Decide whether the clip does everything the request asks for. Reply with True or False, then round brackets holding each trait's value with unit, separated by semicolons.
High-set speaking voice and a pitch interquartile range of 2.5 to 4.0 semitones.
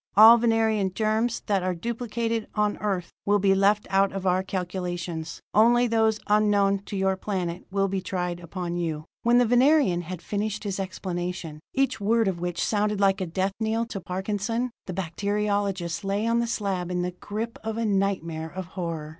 True (195 Hz; 3.3 semitones)